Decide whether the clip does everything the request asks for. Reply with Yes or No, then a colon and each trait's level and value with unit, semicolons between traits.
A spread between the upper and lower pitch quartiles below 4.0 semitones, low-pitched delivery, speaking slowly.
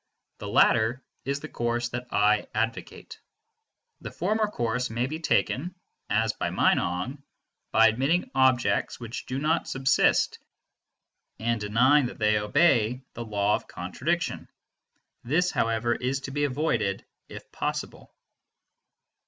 Yes: average, 3.6 semitones; low, 120 Hz; slow, 130 wpm